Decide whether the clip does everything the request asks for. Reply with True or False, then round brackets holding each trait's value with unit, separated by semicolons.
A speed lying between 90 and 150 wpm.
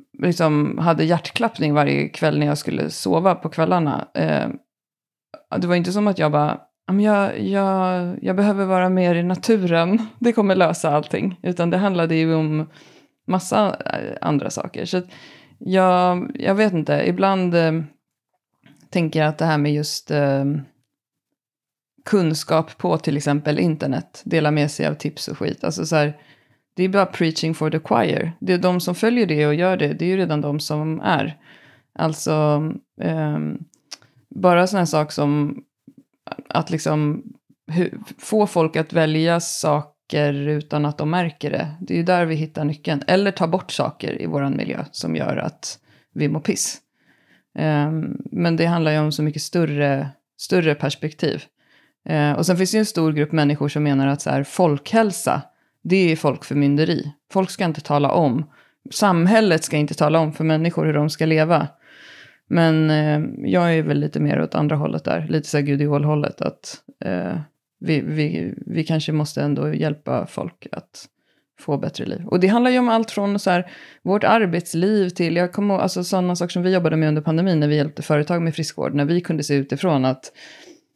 False (175 wpm)